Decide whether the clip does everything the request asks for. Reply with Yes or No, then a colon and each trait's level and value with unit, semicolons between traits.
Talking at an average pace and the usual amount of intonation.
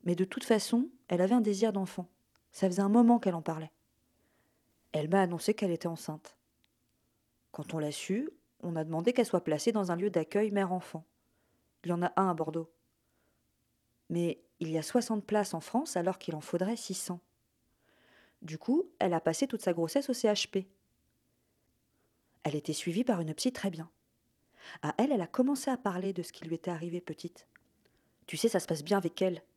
Yes: average, 195 wpm; average, 4.4 semitones